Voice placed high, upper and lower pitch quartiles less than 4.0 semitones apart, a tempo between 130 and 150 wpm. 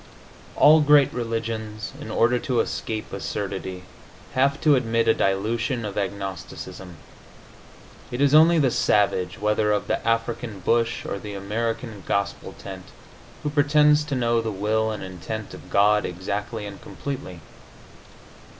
No: low, 110 Hz; average, 3.6 semitones; average, 140 wpm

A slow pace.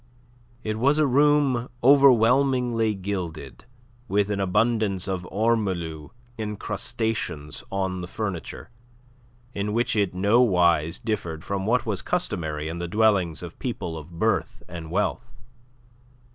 Yes: slow, 120 wpm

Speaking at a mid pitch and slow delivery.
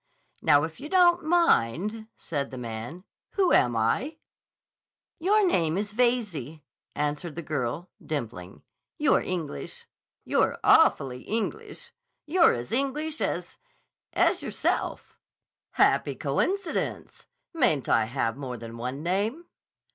Yes: medium, 170 Hz; slow, 115 wpm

